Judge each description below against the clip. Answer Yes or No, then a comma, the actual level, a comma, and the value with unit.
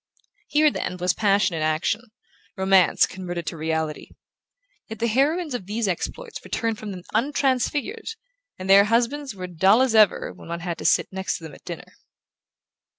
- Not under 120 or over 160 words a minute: No, average, 175 wpm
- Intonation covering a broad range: Yes, wide, 5.7 semitones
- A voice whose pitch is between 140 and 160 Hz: No, high, 200 Hz